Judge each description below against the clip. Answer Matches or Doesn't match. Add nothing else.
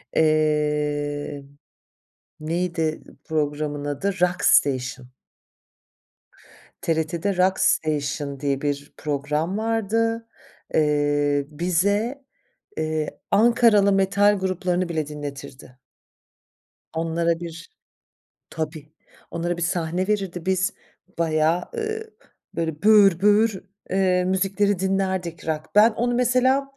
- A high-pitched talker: Doesn't match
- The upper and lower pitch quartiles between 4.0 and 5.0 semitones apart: Matches